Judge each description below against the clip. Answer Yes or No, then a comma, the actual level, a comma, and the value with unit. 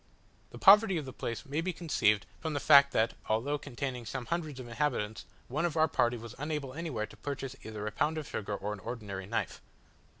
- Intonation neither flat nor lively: No, wide, 5.7 semitones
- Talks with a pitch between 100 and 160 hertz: Yes, low, 135 Hz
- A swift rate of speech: Yes, fast, 210 wpm